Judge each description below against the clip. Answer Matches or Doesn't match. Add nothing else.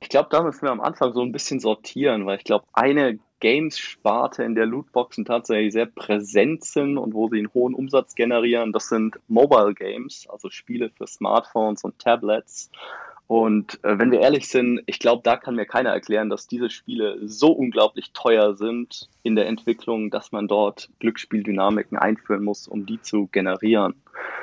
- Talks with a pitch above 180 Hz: Doesn't match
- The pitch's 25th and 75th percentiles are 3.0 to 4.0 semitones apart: Doesn't match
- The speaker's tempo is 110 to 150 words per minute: Doesn't match